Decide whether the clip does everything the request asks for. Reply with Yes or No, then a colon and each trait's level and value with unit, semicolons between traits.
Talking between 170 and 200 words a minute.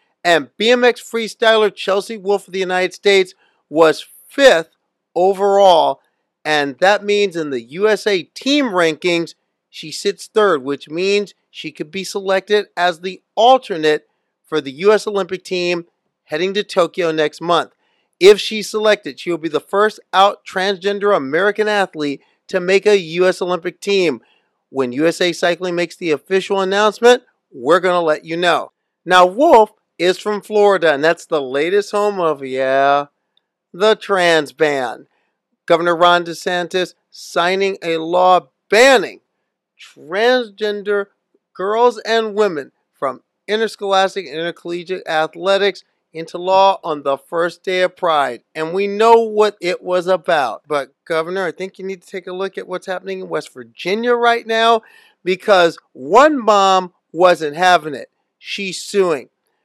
No: average, 145 wpm